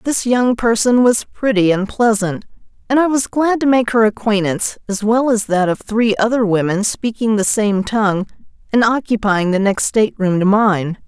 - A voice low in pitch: No, high, 215 Hz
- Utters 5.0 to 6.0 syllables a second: No, 4.8 syllables/s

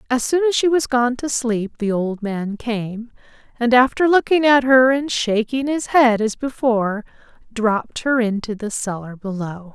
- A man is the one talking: No, female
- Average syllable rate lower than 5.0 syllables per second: Yes, 4.4 syllables/s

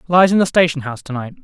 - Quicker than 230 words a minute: Yes, fast, 290 wpm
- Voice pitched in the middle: Yes, medium, 155 Hz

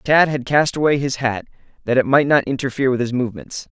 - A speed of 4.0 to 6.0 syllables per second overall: No, 6.2 syllables/s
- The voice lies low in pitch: Yes, low, 130 Hz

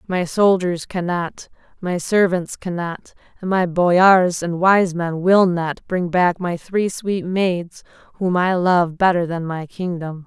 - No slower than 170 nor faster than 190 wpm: No, average, 160 wpm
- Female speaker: Yes, female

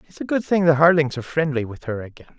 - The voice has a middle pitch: Yes, medium, 145 Hz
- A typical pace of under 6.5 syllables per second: No, 6.8 syllables/s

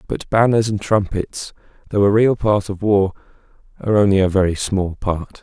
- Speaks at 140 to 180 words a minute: Yes, average, 175 wpm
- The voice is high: No, low, 100 Hz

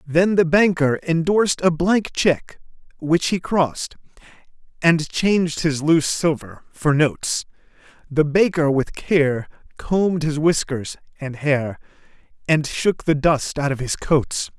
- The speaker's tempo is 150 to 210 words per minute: No, average, 140 wpm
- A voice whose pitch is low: No, medium, 155 Hz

